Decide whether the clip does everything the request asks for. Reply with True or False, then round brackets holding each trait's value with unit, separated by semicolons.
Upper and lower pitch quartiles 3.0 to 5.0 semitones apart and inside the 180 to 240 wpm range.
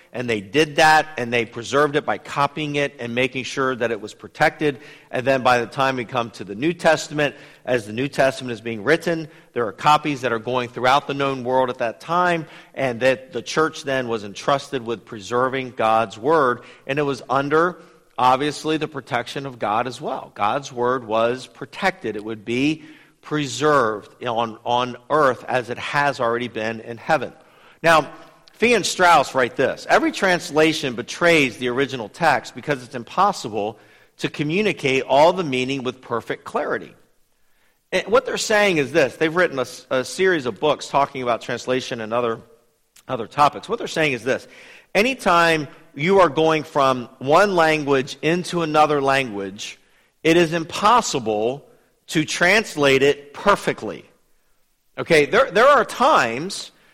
False (4.2 semitones; 165 wpm)